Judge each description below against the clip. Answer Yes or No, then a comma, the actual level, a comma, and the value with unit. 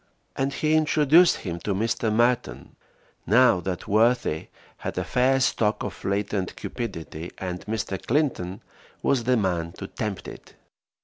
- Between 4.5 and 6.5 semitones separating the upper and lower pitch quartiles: Yes, average, 5.2 semitones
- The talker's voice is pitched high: No, low, 110 Hz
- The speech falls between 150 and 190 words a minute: No, average, 140 wpm